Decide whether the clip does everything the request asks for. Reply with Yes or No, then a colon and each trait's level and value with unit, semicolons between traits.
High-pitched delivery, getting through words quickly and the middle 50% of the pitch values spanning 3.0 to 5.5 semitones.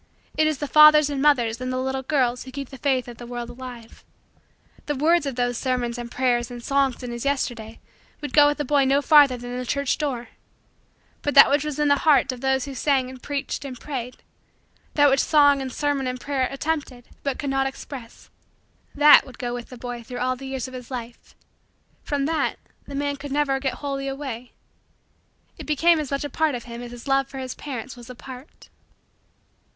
No: very high, 265 Hz; fast, 215 wpm; narrow, 2.5 semitones